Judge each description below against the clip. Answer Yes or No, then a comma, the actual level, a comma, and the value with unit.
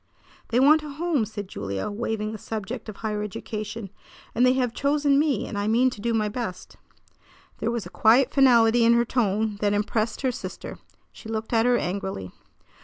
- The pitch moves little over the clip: No, average, 3.0 semitones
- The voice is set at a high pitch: Yes, high, 225 Hz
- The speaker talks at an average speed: Yes, average, 190 wpm